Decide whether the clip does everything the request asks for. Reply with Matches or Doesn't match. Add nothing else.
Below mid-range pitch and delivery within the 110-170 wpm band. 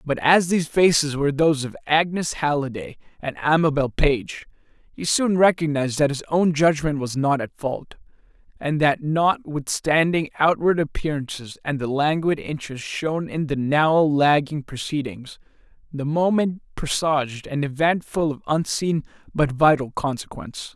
Doesn't match